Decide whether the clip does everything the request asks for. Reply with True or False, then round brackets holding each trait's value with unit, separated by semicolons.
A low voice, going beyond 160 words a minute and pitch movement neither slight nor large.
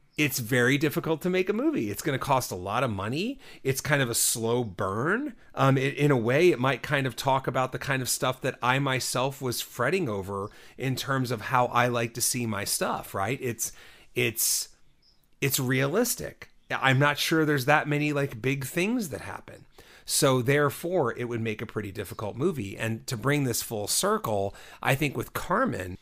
True (130 Hz; 200 wpm; 3.8 semitones)